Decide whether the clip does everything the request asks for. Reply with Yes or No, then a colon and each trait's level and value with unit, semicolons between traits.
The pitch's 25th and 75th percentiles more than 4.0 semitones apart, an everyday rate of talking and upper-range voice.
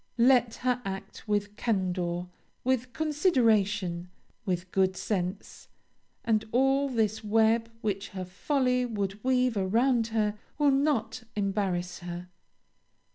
No: average, 4.7 semitones; slow, 115 wpm; high, 215 Hz